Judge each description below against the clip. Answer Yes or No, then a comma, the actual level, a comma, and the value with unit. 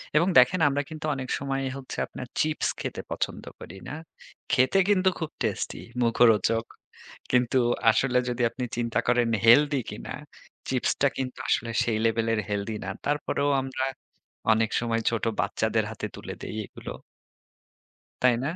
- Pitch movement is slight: No, average, 3.2 semitones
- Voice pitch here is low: Yes, low, 125 Hz